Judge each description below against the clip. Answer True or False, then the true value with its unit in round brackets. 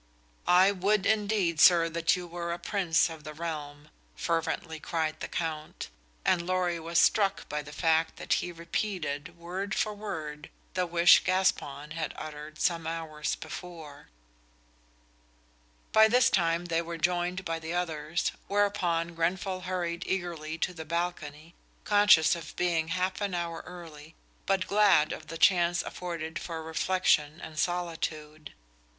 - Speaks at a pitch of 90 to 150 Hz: False (170 Hz)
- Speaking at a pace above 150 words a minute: False (145 wpm)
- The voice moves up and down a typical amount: False (2.2 semitones)